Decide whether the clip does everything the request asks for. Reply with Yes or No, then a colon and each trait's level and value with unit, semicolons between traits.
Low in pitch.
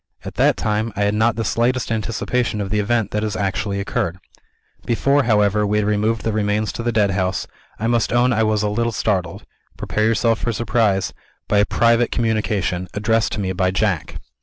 Yes: low, 105 Hz